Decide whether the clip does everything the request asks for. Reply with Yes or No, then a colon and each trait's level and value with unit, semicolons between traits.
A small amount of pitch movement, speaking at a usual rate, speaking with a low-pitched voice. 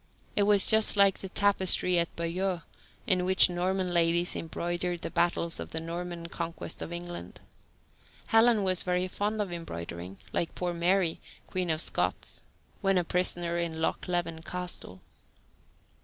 No: narrow, 1.8 semitones; average, 150 wpm; medium, 175 Hz